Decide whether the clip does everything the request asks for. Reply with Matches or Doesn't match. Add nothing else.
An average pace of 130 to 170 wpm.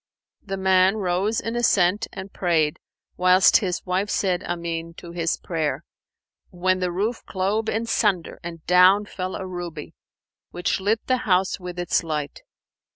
Matches